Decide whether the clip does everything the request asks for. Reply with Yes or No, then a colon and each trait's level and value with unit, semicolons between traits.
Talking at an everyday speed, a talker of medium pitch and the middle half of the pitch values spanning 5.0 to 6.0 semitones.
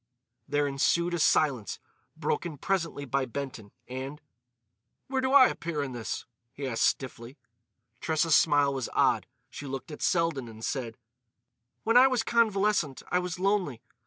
Yes: average, 150 wpm; medium, 145 Hz; average, 5.3 semitones